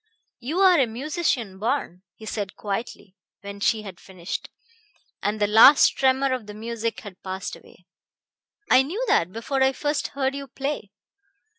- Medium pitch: No, high, 230 Hz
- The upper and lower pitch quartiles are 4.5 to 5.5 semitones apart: Yes, average, 5.2 semitones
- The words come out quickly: No, average, 160 wpm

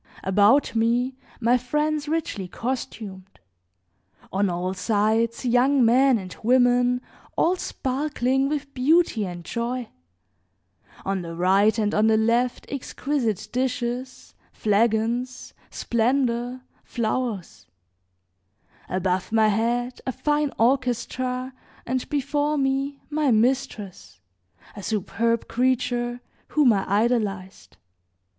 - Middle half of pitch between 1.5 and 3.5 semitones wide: Yes, average, 3.2 semitones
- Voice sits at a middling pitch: No, high, 240 Hz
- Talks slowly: Yes, slow, 100 wpm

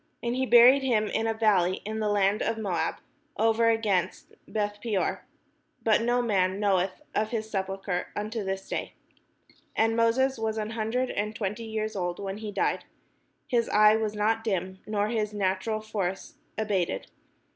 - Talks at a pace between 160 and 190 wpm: Yes, average, 165 wpm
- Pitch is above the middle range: Yes, high, 215 Hz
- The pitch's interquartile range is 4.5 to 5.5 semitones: No, narrow, 2.4 semitones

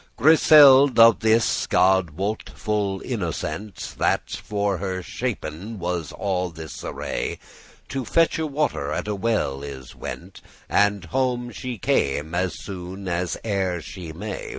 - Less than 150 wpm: Yes, average, 140 wpm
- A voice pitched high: No, low, 100 Hz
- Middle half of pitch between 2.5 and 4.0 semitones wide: No, average, 4.7 semitones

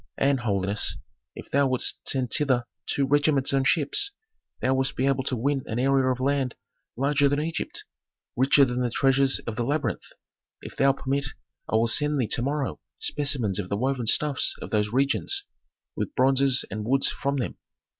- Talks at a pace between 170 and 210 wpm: Yes, average, 180 wpm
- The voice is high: No, low, 135 Hz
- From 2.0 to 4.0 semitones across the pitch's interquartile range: Yes, narrow, 2.4 semitones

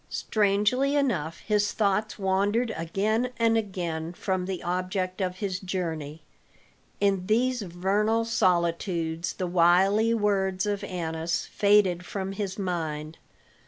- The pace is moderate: No, slow, 120 wpm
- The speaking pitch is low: No, high, 190 Hz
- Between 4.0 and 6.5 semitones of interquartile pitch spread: No, average, 3.1 semitones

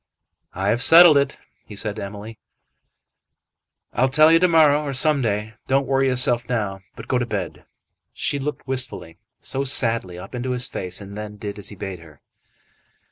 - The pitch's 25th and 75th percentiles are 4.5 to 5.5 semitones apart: Yes, average, 4.9 semitones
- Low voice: Yes, low, 120 Hz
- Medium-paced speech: Yes, average, 185 wpm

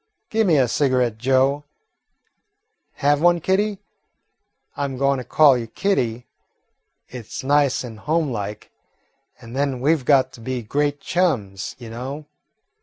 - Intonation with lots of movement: No, average, 3.3 semitones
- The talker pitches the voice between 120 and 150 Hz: Yes, low, 135 Hz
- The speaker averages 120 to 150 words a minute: Yes, average, 145 wpm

